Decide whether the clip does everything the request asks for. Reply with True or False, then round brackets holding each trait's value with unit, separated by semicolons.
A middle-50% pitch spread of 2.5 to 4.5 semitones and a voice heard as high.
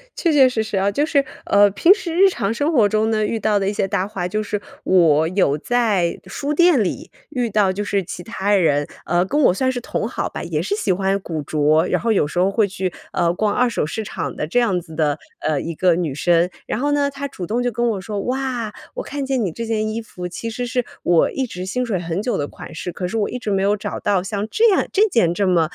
False (5.3 semitones; 205 Hz)